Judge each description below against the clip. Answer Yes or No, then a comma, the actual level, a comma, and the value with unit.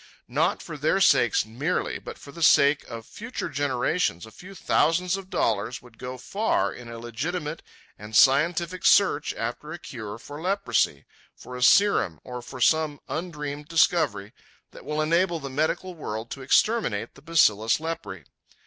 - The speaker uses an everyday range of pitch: No, wide, 6.3 semitones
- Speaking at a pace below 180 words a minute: Yes, average, 160 wpm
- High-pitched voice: No, medium, 145 Hz